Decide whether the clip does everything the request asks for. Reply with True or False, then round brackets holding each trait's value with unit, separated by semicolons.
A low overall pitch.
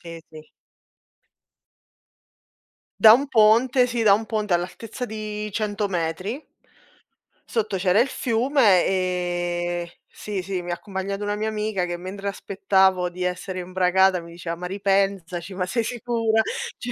False (195 Hz)